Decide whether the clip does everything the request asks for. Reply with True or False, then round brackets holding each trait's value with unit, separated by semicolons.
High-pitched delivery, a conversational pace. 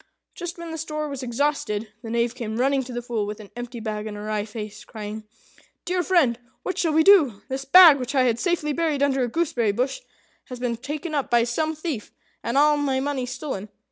False (260 Hz; 220 wpm)